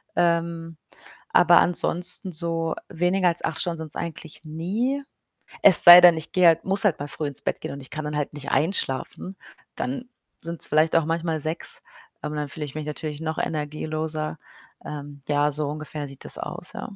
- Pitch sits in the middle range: Yes, medium, 160 Hz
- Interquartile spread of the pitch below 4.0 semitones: Yes, narrow, 2.4 semitones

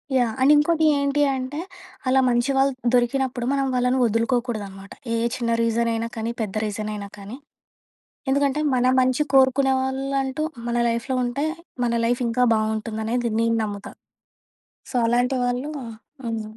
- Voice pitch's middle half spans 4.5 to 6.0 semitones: No, average, 2.7 semitones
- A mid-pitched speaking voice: No, high, 245 Hz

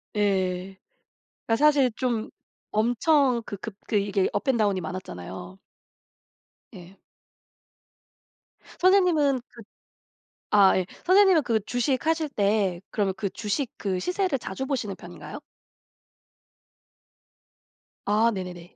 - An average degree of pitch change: No, wide, 6.1 semitones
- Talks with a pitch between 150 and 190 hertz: No, high, 215 Hz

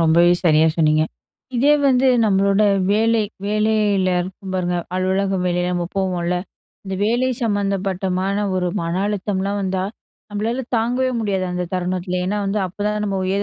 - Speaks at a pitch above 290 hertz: No, high, 195 Hz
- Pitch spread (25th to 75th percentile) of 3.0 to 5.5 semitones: No, narrow, 2.5 semitones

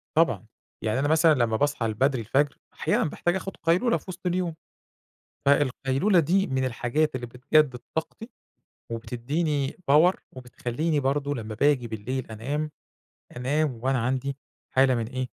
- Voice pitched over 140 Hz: No, low, 135 Hz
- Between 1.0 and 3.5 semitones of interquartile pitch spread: No, average, 4.0 semitones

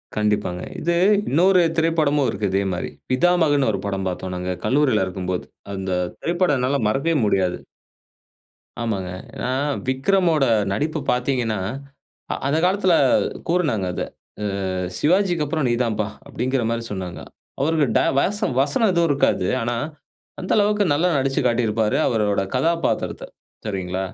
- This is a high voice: No, low, 130 Hz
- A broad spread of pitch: Yes, wide, 8.2 semitones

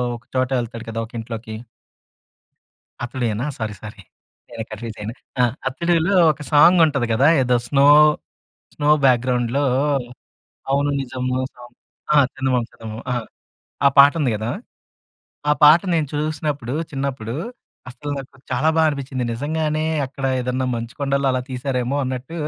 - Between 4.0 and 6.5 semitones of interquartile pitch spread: No, average, 3.2 semitones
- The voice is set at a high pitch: No, low, 130 Hz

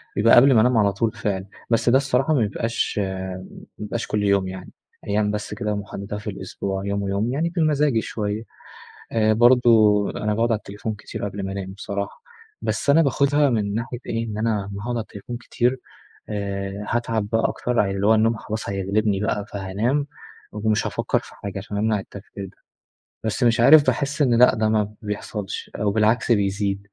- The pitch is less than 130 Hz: Yes, low, 105 Hz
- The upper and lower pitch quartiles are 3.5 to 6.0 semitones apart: No, average, 2.8 semitones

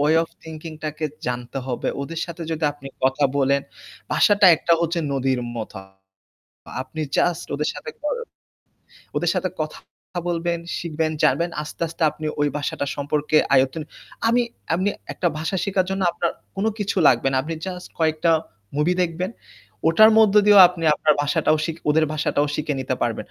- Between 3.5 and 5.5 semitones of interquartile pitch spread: No, average, 3.1 semitones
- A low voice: No, medium, 160 Hz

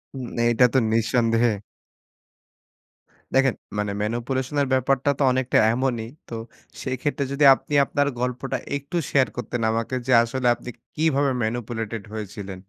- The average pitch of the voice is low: Yes, low, 125 Hz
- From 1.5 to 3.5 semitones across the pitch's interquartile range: Yes, average, 2.8 semitones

